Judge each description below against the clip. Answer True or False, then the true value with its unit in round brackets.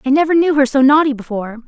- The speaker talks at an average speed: False (250 wpm)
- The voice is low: False (275 Hz)